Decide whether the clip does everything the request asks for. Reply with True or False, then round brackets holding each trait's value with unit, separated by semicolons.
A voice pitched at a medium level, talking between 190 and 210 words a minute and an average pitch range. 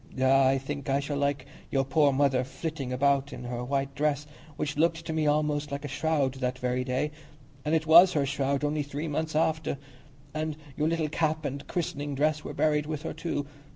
False (145 Hz; 205 wpm; 2.2 semitones)